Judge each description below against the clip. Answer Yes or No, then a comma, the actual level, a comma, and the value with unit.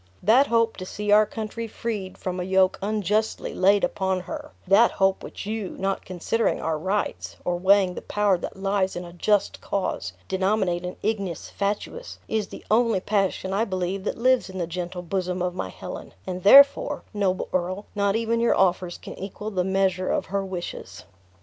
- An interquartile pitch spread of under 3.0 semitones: Yes, narrow, 2.5 semitones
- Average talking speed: Yes, average, 185 wpm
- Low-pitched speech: No, high, 195 Hz